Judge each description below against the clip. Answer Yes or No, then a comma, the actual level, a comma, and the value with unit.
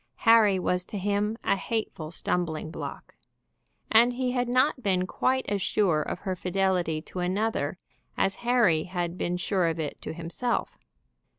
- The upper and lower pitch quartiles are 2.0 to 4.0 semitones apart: No, average, 4.4 semitones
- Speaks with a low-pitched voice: No, high, 190 Hz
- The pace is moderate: Yes, average, 160 wpm